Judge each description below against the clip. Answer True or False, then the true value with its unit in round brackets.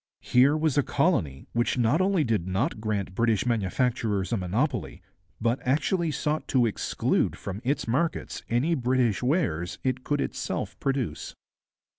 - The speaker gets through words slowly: False (145 wpm)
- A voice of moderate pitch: False (125 Hz)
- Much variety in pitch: False (4.9 semitones)